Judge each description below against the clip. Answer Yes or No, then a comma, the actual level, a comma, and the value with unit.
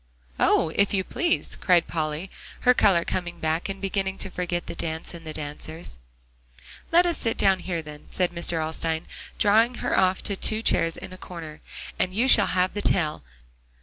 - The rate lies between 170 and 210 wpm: Yes, average, 185 wpm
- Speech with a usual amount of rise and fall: Yes, average, 3.3 semitones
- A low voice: No, medium, 180 Hz